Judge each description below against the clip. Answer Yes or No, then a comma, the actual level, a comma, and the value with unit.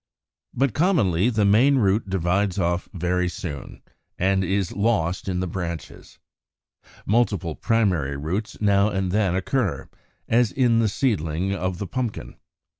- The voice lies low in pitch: Yes, very low, 95 Hz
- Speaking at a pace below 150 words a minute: Yes, slow, 135 wpm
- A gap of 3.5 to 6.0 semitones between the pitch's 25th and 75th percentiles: Yes, average, 3.8 semitones